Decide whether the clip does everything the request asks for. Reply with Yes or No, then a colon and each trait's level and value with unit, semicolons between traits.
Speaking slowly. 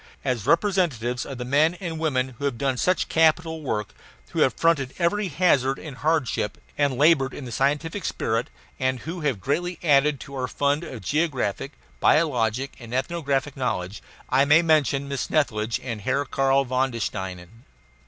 No: average, 170 wpm